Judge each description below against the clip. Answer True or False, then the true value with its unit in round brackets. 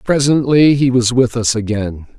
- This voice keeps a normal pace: True (165 wpm)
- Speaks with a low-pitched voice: True (125 Hz)